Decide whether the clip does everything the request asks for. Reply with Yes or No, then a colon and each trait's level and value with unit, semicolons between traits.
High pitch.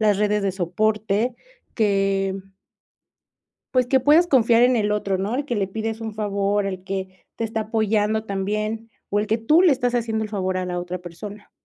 Yes: high, 210 Hz